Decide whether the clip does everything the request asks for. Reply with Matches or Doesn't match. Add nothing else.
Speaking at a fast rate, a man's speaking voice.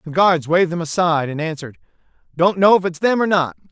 Matches